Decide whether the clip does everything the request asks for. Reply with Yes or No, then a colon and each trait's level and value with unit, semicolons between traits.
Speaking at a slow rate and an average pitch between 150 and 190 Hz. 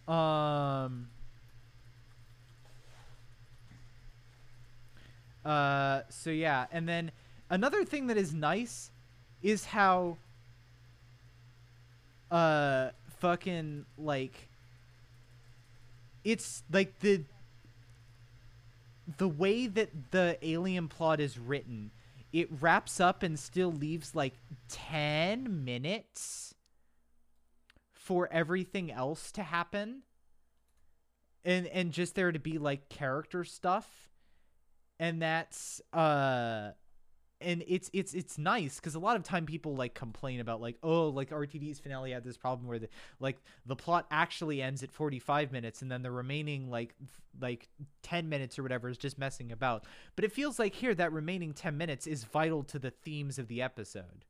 No: slow, 130 wpm; low, 135 Hz